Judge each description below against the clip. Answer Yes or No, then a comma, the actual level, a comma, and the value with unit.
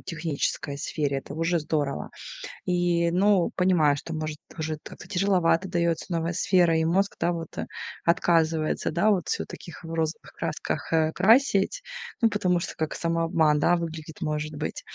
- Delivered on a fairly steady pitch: Yes, narrow, 2.2 semitones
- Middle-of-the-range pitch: Yes, medium, 165 Hz